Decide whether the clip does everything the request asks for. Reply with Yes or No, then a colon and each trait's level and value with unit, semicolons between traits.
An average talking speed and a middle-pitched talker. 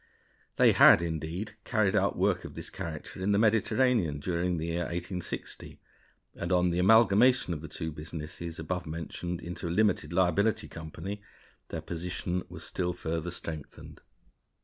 No: average, 150 wpm; very low, 90 Hz